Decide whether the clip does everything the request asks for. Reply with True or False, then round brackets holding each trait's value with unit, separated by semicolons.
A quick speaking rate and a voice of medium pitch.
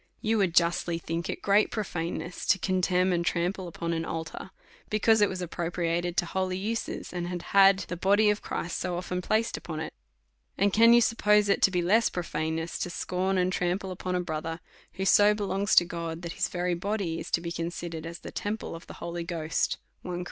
True (215 wpm; 180 Hz)